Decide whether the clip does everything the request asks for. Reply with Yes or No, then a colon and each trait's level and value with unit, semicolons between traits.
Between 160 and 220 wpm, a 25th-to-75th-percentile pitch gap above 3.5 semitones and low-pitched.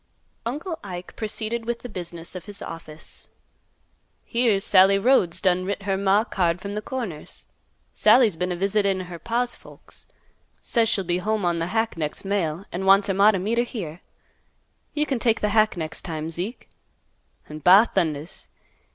No: average, 175 wpm; average, 4.0 semitones; high, 195 Hz